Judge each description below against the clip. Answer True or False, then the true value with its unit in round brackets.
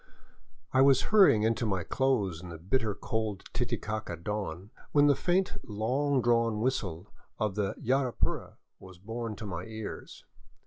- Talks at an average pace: True (160 wpm)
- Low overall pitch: True (110 Hz)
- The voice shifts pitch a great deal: False (5.0 semitones)